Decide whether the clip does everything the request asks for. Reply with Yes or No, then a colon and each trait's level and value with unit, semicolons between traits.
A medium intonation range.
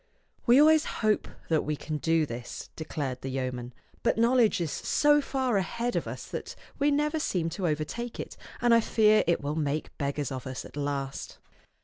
No: wide, 8.9 semitones